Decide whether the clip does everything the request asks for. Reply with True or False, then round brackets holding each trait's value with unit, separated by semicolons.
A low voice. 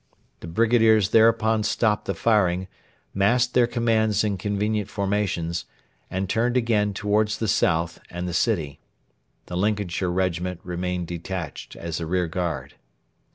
True (100 Hz)